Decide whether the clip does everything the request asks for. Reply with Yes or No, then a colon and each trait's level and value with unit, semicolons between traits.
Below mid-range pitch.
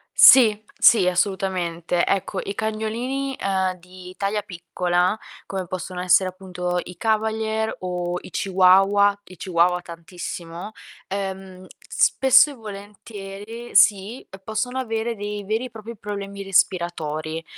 No: high, 195 Hz